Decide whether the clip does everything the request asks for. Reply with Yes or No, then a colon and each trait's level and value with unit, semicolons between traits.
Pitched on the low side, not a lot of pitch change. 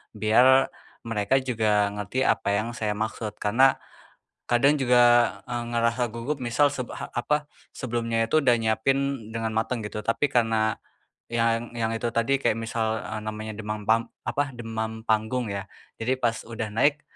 Yes: low, 115 Hz; narrow, 2.1 semitones